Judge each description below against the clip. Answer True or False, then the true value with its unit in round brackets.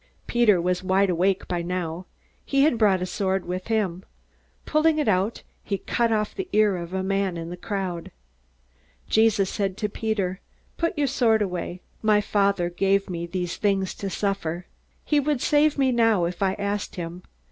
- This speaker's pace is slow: False (180 wpm)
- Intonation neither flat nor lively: True (3.4 semitones)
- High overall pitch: True (195 Hz)